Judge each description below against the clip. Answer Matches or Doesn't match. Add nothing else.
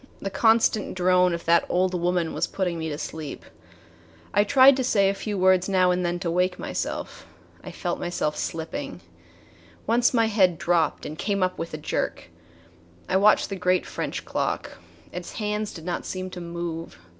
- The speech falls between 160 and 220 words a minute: Matches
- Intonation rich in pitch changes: Doesn't match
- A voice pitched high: Doesn't match